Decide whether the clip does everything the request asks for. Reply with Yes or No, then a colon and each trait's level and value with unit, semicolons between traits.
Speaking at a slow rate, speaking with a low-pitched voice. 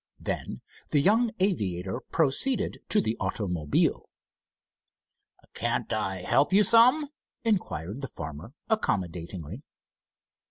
Yes: slow, 95 wpm; low, 120 Hz